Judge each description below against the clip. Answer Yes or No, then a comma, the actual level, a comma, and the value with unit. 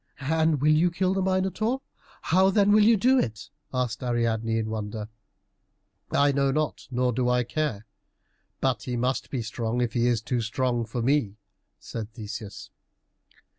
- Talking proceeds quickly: No, average, 165 wpm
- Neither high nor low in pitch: No, low, 125 Hz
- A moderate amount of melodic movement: No, wide, 5.7 semitones